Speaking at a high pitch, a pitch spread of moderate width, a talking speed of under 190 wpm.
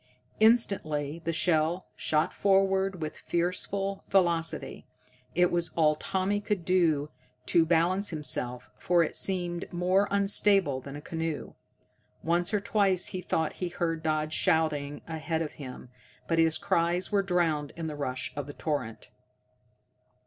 No: medium, 170 Hz; average, 3.3 semitones; average, 140 wpm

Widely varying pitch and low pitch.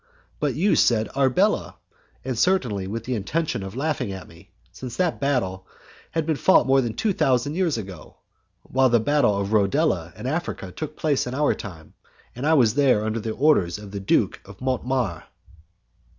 Yes: wide, 6.2 semitones; low, 125 Hz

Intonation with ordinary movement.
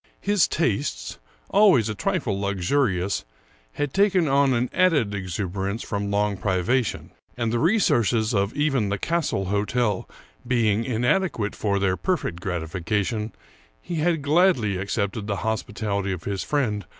No: wide, 6.0 semitones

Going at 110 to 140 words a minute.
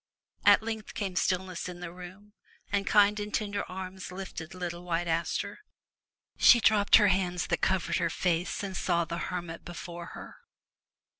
No: average, 160 wpm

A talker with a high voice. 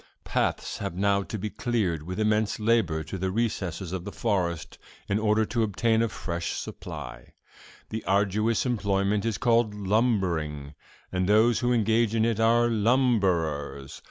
No: low, 105 Hz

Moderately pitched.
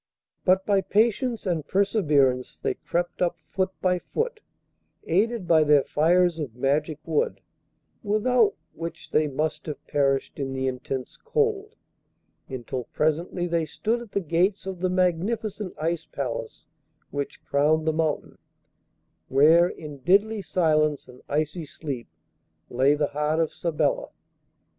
Yes: medium, 165 Hz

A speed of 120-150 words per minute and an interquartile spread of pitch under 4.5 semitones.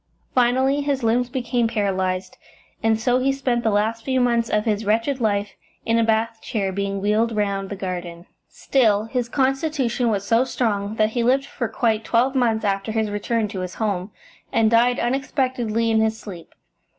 No: average, 180 wpm; average, 3.1 semitones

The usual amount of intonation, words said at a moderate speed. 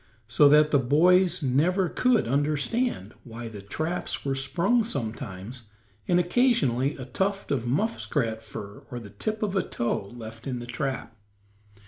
No: wide, 7.3 semitones; average, 150 wpm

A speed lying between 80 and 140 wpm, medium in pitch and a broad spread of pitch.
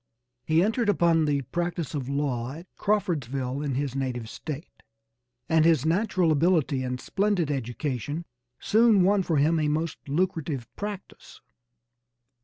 No: slow, 135 wpm; medium, 155 Hz; average, 4.4 semitones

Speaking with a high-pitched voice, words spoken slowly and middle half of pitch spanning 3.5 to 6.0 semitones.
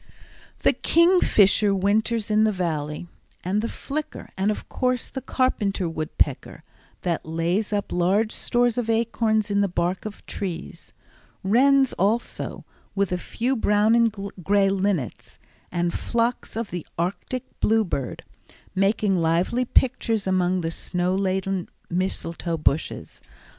Yes: high, 200 Hz; slow, 130 wpm; average, 4.1 semitones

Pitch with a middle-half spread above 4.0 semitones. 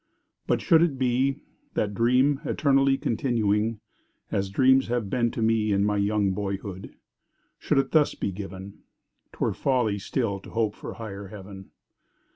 Yes: average, 4.5 semitones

